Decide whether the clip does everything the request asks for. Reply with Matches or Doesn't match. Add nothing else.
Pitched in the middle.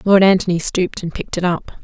Matches